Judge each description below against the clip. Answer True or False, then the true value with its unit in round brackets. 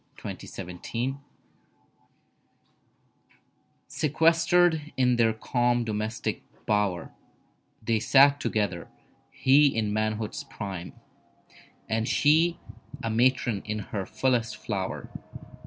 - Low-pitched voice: True (115 Hz)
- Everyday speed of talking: False (90 wpm)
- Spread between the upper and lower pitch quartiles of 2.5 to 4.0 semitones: False (4.4 semitones)